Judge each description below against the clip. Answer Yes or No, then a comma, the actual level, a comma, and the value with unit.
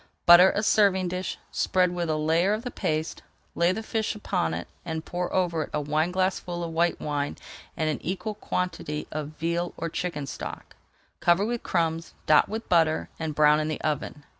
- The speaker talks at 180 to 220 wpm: Yes, average, 190 wpm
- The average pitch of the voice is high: No, medium, 170 Hz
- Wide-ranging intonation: No, average, 3.0 semitones